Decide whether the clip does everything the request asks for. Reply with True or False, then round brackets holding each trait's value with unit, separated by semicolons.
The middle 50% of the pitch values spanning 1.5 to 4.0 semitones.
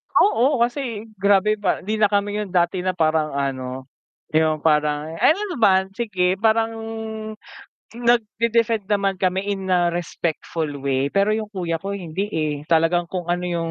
False (4.5 semitones)